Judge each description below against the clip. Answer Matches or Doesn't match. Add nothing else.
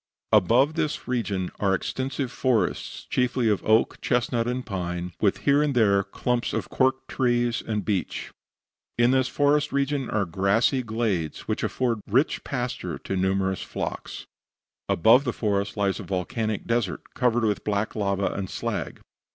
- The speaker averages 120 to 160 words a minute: Matches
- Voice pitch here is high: Doesn't match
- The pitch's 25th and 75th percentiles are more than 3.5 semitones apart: Matches